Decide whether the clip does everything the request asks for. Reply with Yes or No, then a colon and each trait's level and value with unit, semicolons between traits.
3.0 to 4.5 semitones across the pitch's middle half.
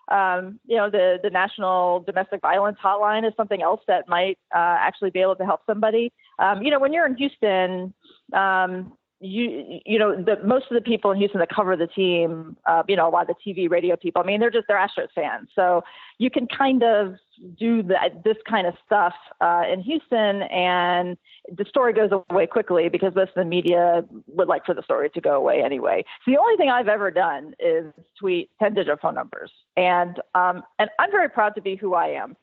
Yes: average, 3.7 semitones